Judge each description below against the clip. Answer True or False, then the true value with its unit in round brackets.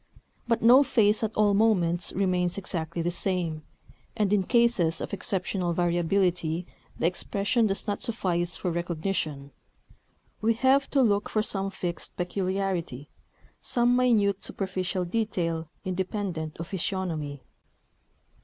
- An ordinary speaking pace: False (125 wpm)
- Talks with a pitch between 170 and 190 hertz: True (185 Hz)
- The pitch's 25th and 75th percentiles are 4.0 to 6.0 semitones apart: False (3.4 semitones)